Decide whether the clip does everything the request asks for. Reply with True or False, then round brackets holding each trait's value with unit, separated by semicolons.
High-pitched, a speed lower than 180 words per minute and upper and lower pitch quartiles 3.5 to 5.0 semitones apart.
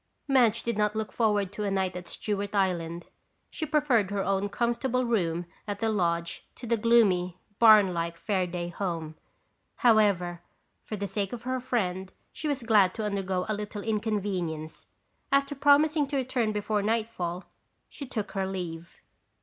True (205 Hz; 160 wpm; 4.2 semitones)